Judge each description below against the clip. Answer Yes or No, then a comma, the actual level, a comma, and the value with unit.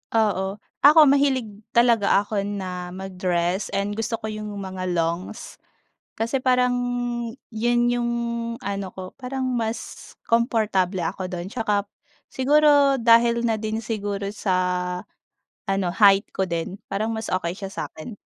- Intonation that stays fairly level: No, average, 3.6 semitones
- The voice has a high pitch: Yes, high, 210 Hz